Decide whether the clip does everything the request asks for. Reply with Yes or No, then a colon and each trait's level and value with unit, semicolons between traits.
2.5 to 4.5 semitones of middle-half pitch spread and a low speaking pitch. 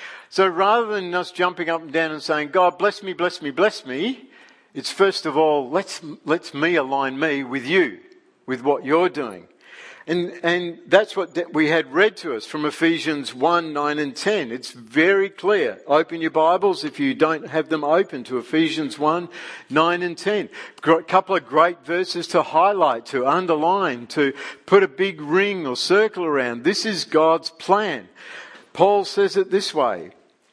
No: average, 4.0 semitones; medium, 170 Hz